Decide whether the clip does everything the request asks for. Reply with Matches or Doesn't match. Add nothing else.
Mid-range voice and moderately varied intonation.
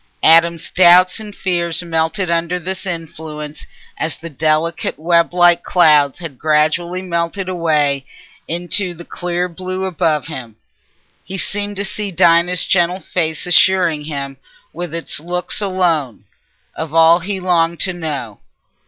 Doesn't match